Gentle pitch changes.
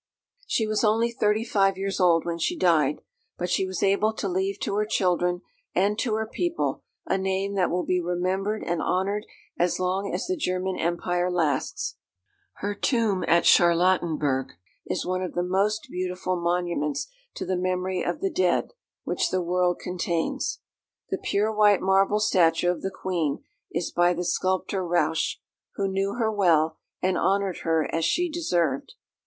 Yes: narrow, 2.3 semitones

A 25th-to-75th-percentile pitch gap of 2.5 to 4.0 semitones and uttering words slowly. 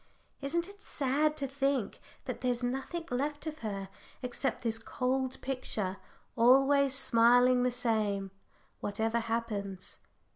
Yes: average, 3.3 semitones; slow, 120 wpm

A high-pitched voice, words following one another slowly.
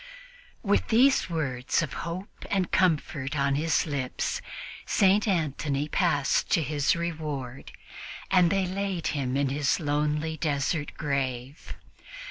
No: medium, 150 Hz; slow, 120 wpm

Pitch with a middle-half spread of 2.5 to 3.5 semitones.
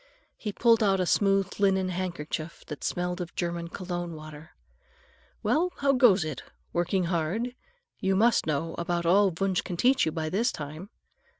Yes: average, 3.0 semitones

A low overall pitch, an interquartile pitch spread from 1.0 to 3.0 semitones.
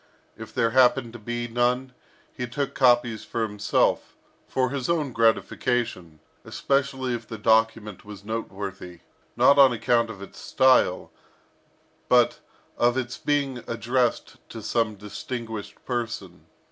Yes: low, 120 Hz; narrow, 2.5 semitones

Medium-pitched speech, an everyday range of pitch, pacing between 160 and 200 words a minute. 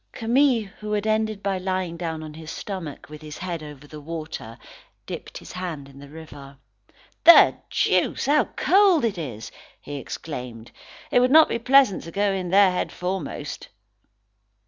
No: medium, 180 Hz; wide, 6.1 semitones; average, 170 wpm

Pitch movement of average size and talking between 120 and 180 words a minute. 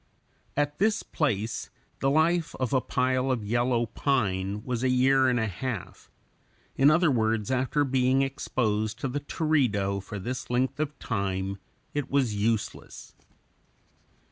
Yes: average, 4.0 semitones; average, 145 wpm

